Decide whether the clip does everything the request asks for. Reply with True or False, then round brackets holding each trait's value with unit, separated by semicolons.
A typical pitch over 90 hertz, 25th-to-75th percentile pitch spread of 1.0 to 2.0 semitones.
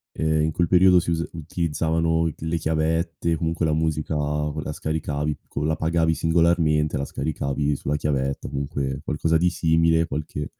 False (80 Hz; 1.7 semitones)